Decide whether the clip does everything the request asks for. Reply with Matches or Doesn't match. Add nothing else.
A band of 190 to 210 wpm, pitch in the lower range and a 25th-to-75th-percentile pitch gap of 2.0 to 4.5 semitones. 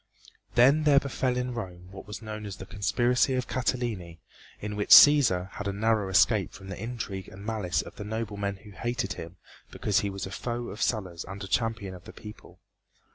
Matches